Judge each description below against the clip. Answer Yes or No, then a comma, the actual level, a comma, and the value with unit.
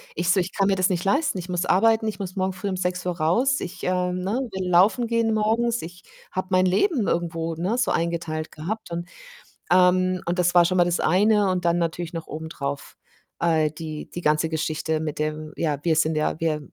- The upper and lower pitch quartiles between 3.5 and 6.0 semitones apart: No, average, 2.8 semitones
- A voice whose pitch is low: No, medium, 180 Hz